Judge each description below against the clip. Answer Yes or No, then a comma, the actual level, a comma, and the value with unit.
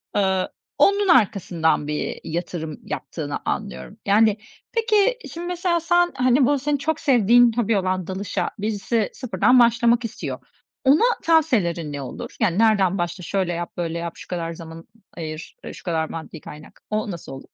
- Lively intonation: Yes, wide, 7.0 semitones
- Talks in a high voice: Yes, high, 200 Hz